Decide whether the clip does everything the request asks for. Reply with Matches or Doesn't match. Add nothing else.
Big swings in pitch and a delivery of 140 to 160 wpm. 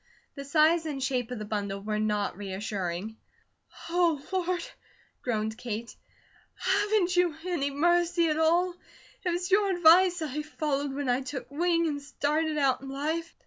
Matches